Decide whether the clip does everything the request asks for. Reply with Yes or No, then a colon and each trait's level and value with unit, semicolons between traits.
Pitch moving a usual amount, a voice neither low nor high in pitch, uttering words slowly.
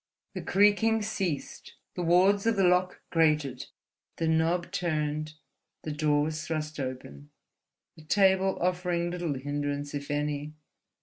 Yes: average, 3.6 semitones; medium, 160 Hz; slow, 125 wpm